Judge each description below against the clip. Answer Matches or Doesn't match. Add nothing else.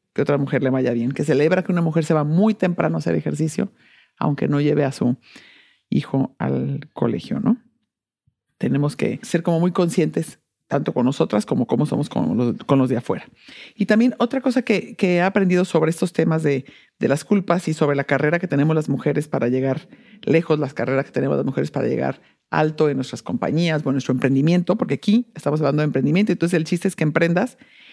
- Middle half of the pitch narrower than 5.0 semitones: Doesn't match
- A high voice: Doesn't match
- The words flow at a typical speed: Doesn't match